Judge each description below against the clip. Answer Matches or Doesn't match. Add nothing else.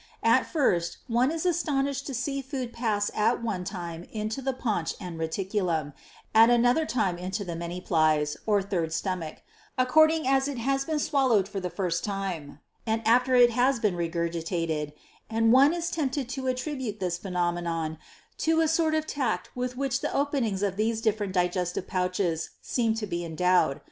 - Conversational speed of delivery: Matches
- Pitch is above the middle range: Matches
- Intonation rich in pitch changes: Matches